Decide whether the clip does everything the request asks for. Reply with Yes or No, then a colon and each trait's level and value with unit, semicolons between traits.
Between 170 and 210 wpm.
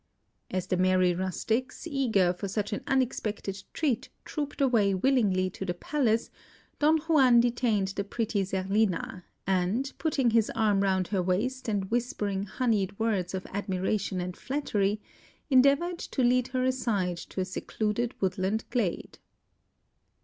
No: average, 140 wpm